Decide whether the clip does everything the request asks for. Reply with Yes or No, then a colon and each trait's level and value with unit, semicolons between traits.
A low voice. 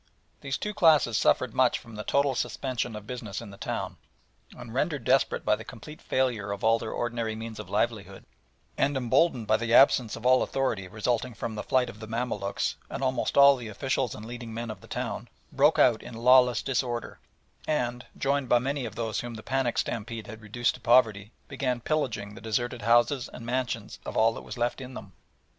Yes: low, 120 Hz